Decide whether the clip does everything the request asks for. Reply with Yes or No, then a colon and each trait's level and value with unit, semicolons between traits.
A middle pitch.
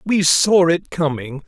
Yes: medium, 165 Hz